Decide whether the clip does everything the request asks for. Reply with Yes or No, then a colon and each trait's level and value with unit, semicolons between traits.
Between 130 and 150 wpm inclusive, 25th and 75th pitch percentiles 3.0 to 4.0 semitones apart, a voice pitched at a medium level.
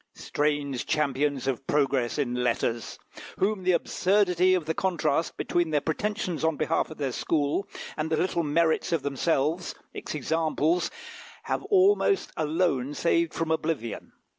Yes: average, 140 wpm; average, 3.5 semitones; medium, 155 Hz